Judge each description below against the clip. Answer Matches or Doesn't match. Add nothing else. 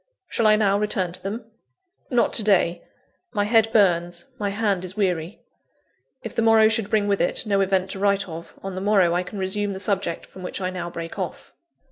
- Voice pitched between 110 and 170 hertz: Doesn't match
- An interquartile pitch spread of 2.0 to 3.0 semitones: Matches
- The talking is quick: Matches